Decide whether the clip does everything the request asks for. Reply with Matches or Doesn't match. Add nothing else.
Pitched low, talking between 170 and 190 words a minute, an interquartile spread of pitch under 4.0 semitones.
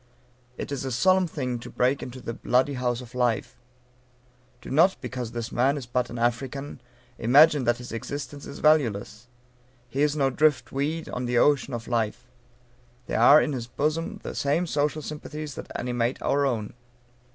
Matches